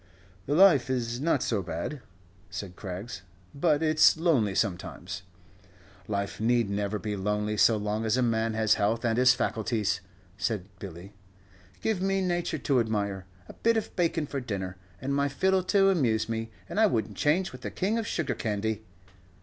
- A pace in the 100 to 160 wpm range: No, average, 175 wpm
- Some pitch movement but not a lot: No, wide, 6.7 semitones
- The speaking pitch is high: No, low, 115 Hz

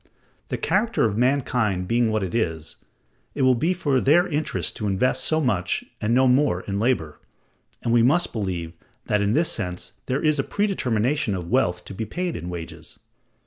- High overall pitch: No, low, 115 Hz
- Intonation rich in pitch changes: Yes, wide, 6.6 semitones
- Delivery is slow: No, average, 185 wpm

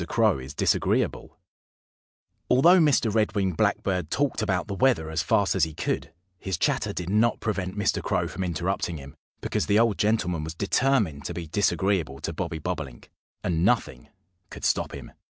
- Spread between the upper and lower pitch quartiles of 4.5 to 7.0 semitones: Yes, average, 4.9 semitones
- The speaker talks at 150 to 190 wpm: Yes, average, 170 wpm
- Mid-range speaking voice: No, very low, 95 Hz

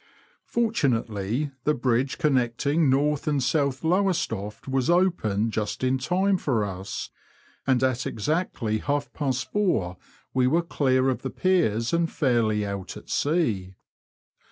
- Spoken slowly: Yes, slow, 130 wpm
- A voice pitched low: Yes, low, 130 Hz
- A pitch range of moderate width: No, wide, 5.8 semitones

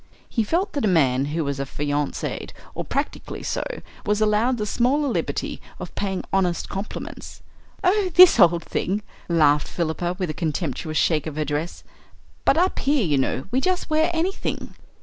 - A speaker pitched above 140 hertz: Yes, medium, 185 Hz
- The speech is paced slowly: No, average, 170 wpm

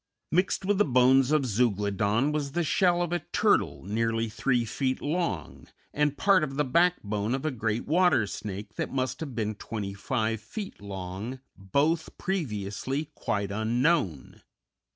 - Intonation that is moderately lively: No, wide, 6.6 semitones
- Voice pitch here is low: Yes, low, 125 Hz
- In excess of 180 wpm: No, average, 150 wpm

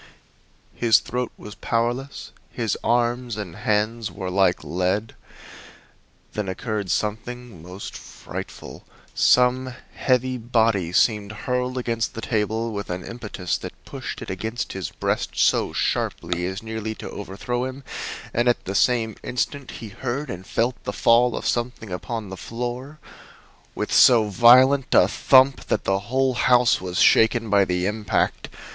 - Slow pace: No, average, 145 wpm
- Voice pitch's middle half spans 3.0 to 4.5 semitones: Yes, average, 3.5 semitones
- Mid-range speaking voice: No, low, 115 Hz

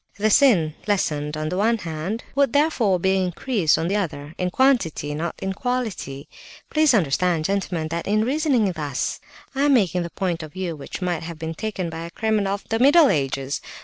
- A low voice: No, medium, 185 Hz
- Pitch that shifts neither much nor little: No, wide, 5.7 semitones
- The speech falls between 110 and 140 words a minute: No, average, 195 wpm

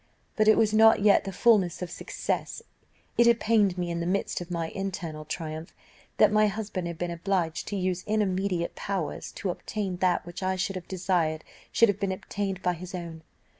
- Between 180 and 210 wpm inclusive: Yes, average, 200 wpm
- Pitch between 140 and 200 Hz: Yes, medium, 185 Hz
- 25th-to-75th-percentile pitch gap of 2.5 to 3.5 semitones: Yes, average, 2.8 semitones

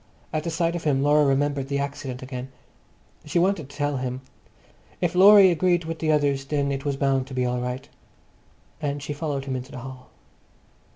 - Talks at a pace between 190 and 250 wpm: Yes, average, 195 wpm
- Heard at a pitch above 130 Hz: Yes, medium, 140 Hz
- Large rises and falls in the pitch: No, average, 2.9 semitones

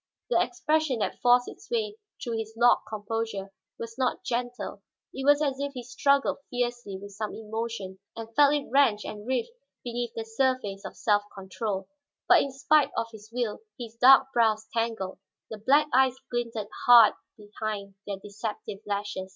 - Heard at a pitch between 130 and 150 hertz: No, high, 230 Hz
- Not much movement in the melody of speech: No, average, 3.6 semitones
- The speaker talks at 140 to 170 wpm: Yes, average, 165 wpm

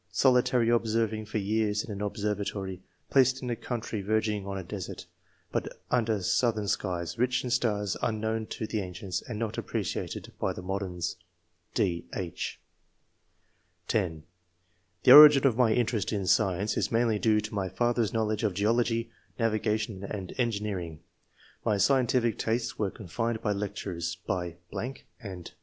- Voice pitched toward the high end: No, low, 105 Hz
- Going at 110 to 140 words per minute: No, average, 150 wpm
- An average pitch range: Yes, average, 3.0 semitones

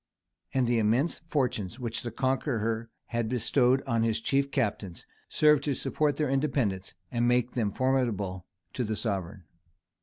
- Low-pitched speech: Yes, low, 120 Hz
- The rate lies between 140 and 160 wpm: Yes, average, 150 wpm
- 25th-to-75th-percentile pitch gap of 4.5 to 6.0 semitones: No, average, 3.6 semitones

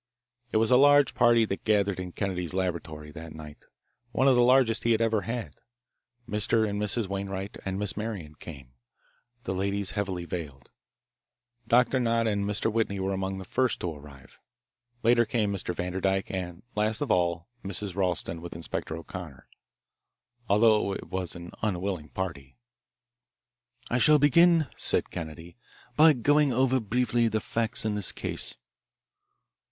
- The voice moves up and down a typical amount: Yes, average, 4.6 semitones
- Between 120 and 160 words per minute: Yes, average, 155 wpm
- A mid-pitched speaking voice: No, low, 100 Hz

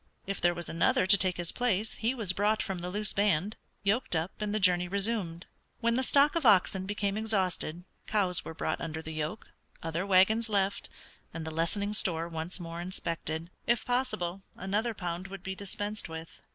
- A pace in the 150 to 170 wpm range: No, average, 190 wpm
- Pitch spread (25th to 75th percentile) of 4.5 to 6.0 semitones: No, average, 3.6 semitones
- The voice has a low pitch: No, high, 190 Hz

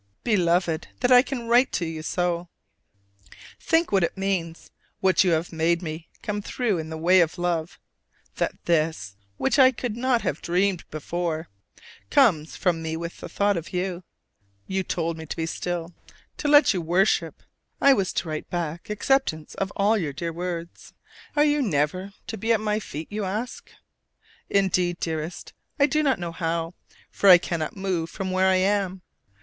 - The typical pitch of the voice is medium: Yes, medium, 180 Hz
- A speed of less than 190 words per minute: Yes, average, 175 wpm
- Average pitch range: Yes, average, 3.9 semitones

